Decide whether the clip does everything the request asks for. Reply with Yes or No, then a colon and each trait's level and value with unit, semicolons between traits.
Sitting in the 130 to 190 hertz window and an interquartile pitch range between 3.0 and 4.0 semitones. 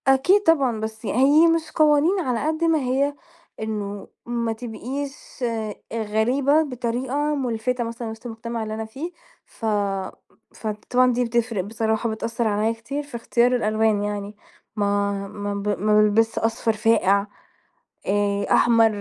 No: high, 230 Hz; average, 3.5 semitones